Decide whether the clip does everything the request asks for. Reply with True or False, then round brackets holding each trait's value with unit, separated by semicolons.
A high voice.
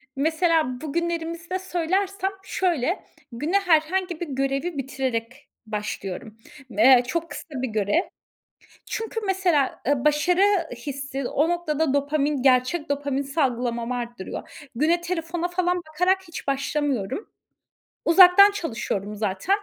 True (300 Hz)